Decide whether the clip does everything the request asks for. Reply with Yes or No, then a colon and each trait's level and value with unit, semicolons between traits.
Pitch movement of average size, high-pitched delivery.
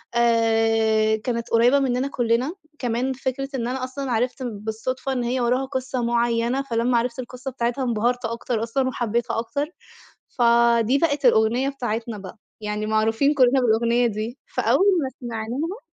No: narrow, 2.3 semitones; high, 240 Hz